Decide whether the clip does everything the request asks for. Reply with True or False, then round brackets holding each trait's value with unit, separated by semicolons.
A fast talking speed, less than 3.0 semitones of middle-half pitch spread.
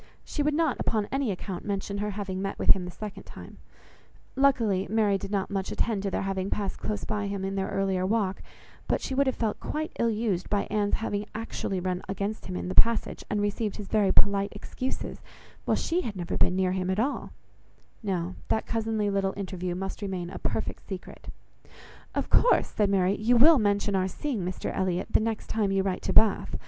True (210 wpm; 2.5 semitones)